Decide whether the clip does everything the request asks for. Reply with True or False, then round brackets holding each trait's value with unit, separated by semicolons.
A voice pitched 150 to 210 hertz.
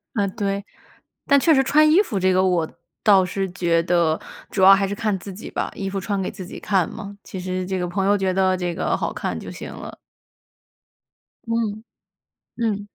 True (195 Hz)